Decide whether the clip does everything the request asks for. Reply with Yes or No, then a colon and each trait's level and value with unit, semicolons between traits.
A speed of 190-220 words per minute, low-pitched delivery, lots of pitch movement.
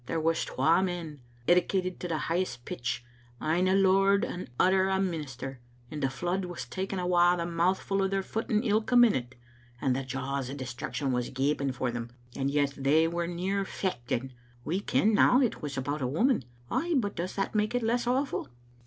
No: average, 195 wpm; medium, 175 Hz; wide, 6.1 semitones